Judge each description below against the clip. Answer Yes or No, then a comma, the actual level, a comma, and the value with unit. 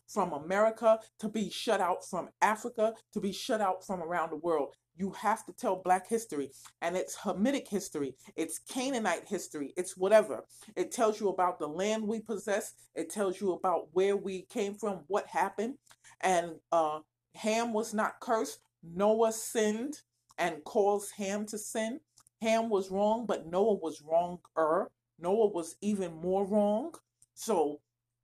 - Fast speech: No, average, 160 wpm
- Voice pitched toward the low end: No, high, 195 Hz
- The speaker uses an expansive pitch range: No, average, 4.3 semitones